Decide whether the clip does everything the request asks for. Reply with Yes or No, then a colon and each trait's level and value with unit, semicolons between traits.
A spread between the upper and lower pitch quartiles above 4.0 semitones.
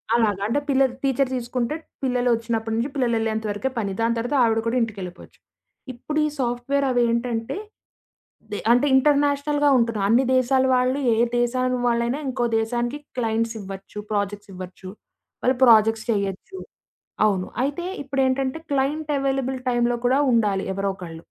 No: average, 3.1 semitones